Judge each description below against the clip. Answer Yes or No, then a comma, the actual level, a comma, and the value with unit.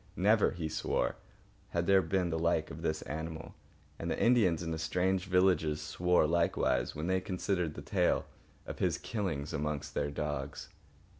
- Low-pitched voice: Yes, very low, 85 Hz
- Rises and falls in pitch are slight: No, average, 3.2 semitones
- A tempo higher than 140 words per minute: Yes, average, 160 wpm